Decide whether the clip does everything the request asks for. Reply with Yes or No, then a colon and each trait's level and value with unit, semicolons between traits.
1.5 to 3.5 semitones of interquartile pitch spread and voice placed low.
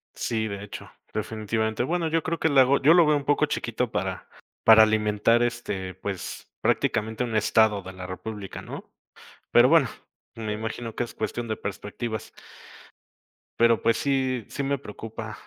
Yes: average, 3.0 semitones; low, 110 Hz